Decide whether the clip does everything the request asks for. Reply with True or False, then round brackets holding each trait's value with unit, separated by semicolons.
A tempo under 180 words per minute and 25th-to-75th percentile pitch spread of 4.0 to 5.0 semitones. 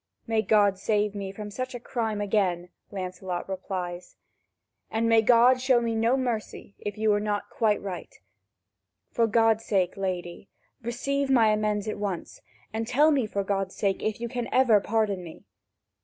False (170 wpm; 2.9 semitones)